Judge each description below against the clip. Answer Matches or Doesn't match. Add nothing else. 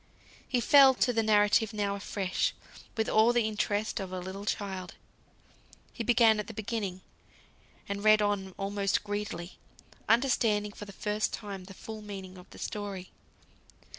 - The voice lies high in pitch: Matches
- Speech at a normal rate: Matches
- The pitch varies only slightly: Matches